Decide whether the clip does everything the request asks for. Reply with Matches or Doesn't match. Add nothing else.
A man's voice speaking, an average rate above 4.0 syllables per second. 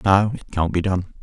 Matches